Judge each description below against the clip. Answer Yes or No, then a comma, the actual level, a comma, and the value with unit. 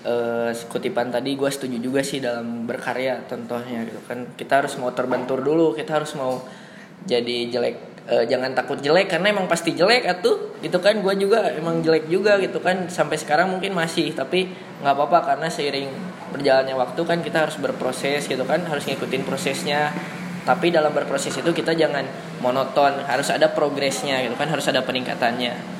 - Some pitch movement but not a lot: Yes, average, 5.0 semitones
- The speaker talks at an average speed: No, fast, 175 wpm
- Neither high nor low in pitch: Yes, medium, 150 Hz